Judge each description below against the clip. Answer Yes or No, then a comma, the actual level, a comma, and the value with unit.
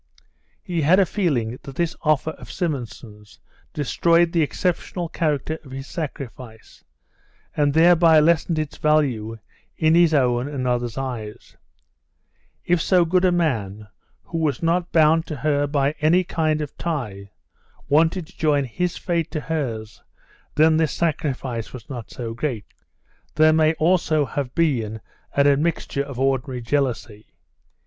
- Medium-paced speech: Yes, average, 145 wpm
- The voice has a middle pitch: Yes, medium, 150 Hz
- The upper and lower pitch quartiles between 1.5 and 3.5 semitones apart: No, average, 4.5 semitones